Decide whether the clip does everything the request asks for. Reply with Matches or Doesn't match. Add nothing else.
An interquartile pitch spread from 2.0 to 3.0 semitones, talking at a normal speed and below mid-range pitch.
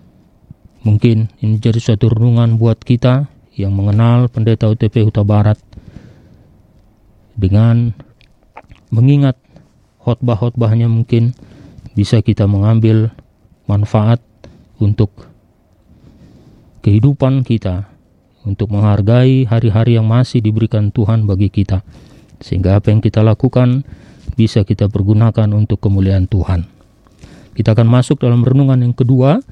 Matches